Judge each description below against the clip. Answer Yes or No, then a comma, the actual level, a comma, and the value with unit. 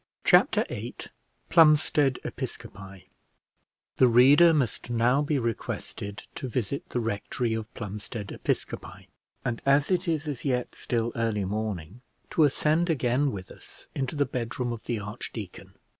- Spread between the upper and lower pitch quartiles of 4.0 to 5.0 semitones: Yes, average, 4.7 semitones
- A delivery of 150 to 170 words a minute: No, average, 140 wpm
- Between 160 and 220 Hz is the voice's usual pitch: No, low, 120 Hz